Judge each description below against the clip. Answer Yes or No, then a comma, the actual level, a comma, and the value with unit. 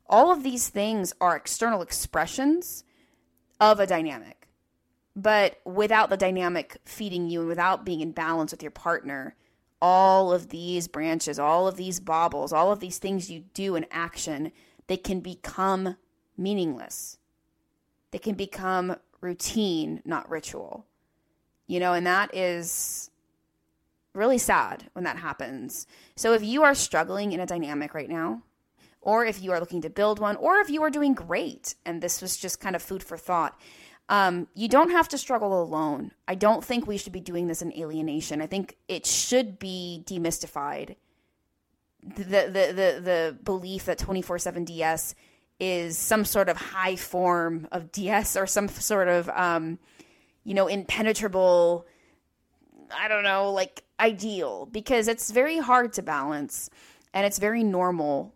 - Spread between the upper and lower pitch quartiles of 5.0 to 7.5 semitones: No, average, 3.9 semitones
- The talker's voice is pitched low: No, medium, 185 Hz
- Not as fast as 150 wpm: No, average, 160 wpm